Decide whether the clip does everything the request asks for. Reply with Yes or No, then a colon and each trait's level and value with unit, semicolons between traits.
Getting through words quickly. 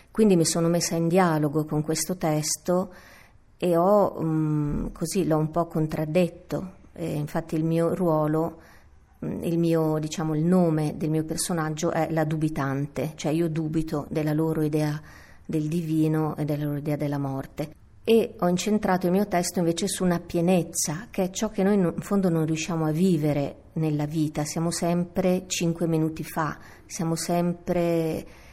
No: average, 160 wpm